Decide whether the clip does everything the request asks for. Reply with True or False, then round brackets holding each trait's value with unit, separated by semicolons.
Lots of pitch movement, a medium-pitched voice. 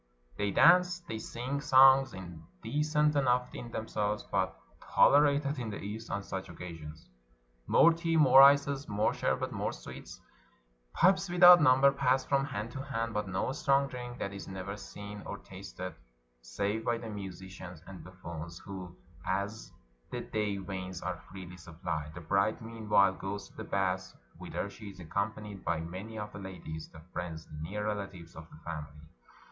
False (6.1 semitones; 105 Hz)